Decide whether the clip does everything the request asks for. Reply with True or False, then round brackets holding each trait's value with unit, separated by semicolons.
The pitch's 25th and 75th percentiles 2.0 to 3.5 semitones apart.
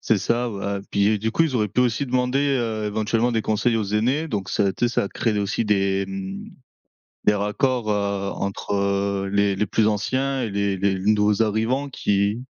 True (2.8 semitones)